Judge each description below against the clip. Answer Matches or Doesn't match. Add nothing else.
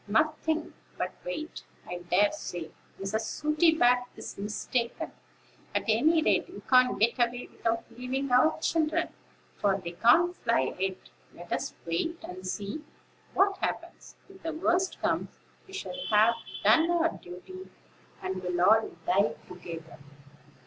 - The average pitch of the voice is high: Matches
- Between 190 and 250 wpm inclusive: Doesn't match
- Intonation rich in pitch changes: Matches